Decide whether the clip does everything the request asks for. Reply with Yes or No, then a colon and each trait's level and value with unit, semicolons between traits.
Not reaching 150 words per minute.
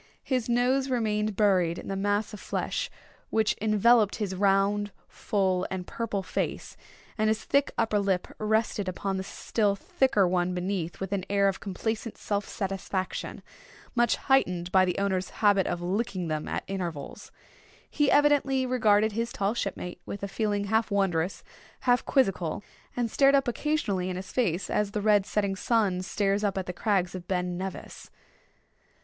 No: average, 165 wpm